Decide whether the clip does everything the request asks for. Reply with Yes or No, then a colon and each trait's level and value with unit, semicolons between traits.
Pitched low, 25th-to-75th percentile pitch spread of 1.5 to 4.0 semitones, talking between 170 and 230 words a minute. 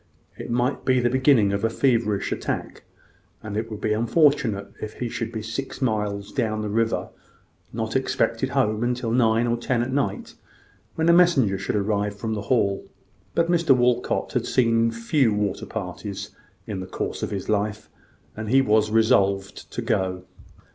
Yes: low, 110 Hz; average, 3.1 semitones; average, 175 wpm